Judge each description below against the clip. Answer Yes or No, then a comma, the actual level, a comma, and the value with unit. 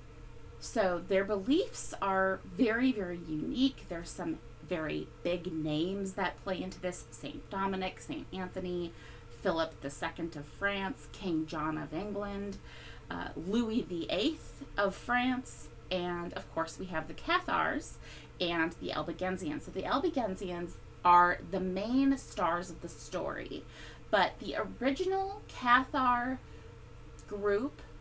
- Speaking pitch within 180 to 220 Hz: Yes, medium, 185 Hz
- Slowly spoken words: Yes, slow, 125 wpm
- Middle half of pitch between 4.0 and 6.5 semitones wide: Yes, average, 4.6 semitones